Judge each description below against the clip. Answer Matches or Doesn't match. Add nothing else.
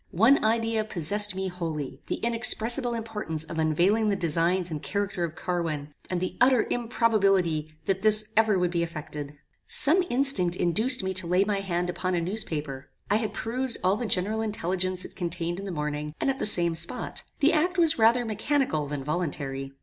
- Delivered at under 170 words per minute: Doesn't match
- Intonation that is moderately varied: Matches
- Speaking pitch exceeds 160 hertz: Matches